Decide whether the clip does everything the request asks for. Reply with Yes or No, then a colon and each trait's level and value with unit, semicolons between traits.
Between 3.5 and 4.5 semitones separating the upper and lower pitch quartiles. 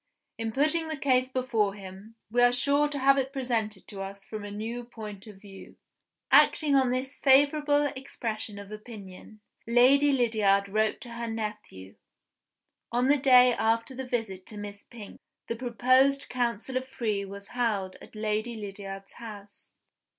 Yes: average, 4.0 semitones